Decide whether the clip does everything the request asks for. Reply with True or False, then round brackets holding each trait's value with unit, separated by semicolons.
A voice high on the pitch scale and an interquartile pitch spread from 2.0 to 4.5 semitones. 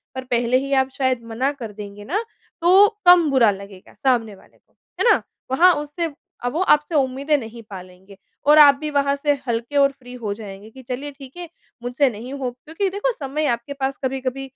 True (265 Hz; 3.8 semitones)